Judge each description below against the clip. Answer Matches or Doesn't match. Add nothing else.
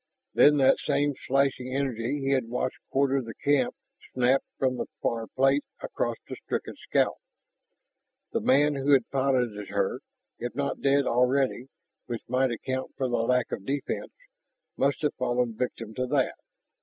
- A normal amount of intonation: Doesn't match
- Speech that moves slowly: Doesn't match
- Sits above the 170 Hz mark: Doesn't match